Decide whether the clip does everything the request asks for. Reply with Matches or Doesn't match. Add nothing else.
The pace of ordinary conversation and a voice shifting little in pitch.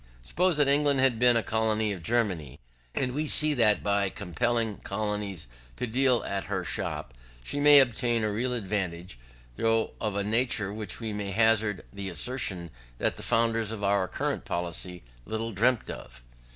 Doesn't match